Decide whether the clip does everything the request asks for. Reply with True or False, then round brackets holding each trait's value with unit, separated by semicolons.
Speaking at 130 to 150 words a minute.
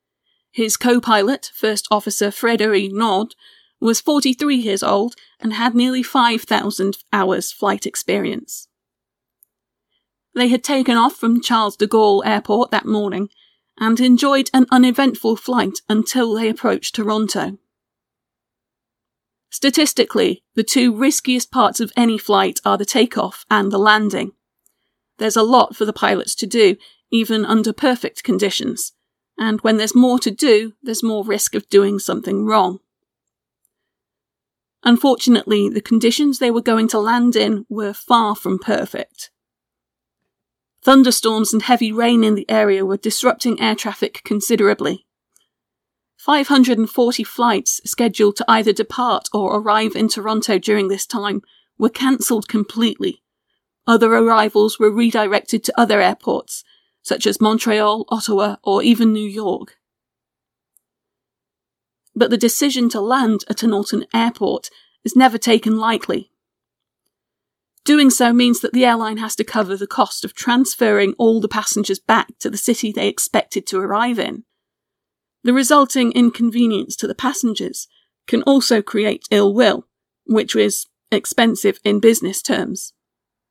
True (135 wpm)